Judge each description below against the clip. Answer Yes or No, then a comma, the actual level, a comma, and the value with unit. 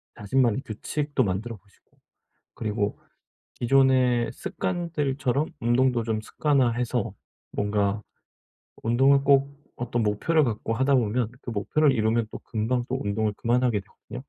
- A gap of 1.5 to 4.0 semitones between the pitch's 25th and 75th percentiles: Yes, average, 3.6 semitones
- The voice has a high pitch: No, low, 120 Hz